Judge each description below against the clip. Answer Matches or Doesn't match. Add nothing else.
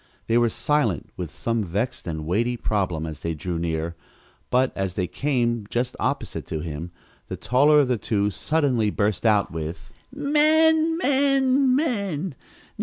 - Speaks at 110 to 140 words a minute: Doesn't match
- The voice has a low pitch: Matches